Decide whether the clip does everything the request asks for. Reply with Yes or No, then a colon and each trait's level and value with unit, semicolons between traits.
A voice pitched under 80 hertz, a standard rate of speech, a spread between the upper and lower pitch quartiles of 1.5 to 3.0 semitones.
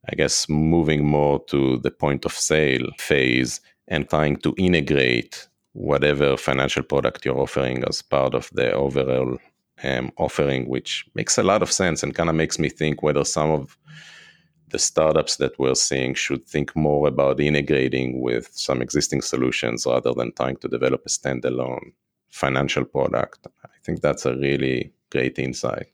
Yes: very low, 70 Hz; average, 165 wpm; narrow, 2.5 semitones